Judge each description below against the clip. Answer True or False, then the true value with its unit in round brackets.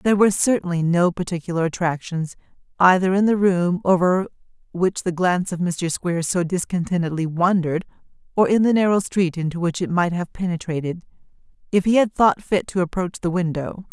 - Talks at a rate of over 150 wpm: True (170 wpm)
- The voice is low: False (180 Hz)